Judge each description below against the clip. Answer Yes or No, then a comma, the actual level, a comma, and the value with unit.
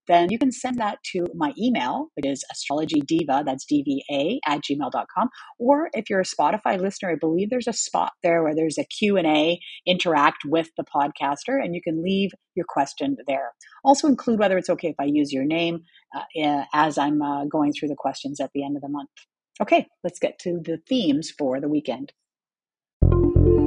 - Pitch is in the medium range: Yes, medium, 175 Hz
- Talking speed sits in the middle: Yes, average, 190 wpm